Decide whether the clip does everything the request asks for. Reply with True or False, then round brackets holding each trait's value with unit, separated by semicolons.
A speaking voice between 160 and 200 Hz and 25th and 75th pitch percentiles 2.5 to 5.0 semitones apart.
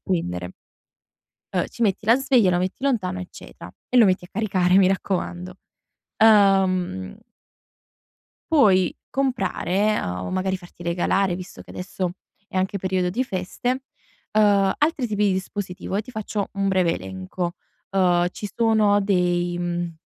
True (190 Hz; 2.8 semitones)